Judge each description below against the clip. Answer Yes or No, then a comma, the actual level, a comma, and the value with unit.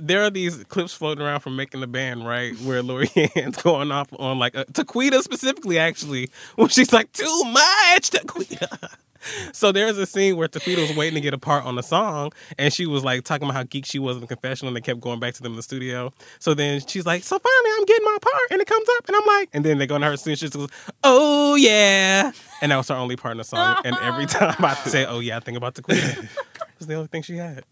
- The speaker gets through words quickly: Yes, fast, 265 wpm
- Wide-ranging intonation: Yes, wide, 8.3 semitones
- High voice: No, medium, 155 Hz